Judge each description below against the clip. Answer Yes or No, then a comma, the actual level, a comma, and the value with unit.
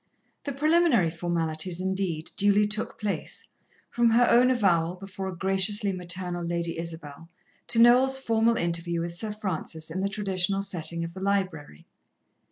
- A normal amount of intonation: Yes, average, 3.9 semitones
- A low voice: No, high, 190 Hz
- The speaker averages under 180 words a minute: Yes, average, 150 wpm